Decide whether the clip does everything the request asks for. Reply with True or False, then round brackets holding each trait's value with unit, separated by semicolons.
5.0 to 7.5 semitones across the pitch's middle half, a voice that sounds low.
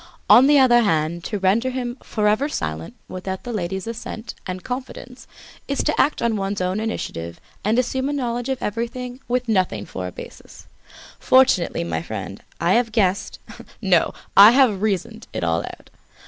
False (5.3 semitones; 220 Hz)